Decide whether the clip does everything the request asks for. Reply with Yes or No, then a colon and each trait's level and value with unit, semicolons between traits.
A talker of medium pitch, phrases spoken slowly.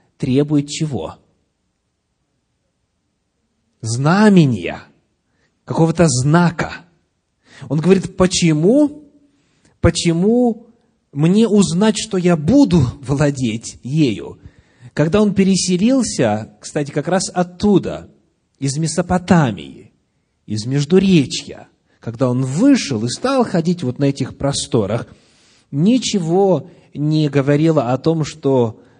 Yes: medium, 160 Hz; slow, 90 wpm